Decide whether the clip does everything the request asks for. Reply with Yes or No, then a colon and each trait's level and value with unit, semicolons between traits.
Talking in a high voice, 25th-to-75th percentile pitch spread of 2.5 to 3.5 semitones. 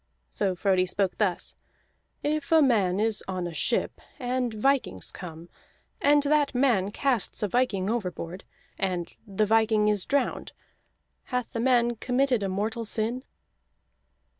No: high, 220 Hz; average, 4.9 semitones